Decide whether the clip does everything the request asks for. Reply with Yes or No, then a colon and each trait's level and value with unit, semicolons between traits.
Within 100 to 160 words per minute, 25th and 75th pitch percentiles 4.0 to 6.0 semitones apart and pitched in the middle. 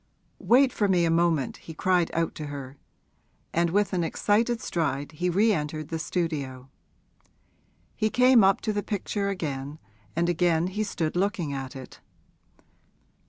Yes: average, 155 wpm; average, 4.7 semitones; medium, 170 Hz